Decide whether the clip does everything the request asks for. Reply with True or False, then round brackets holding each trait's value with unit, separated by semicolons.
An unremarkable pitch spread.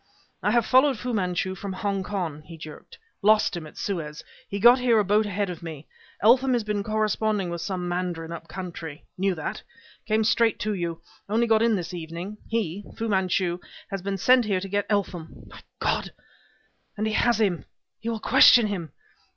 True (3.8 semitones)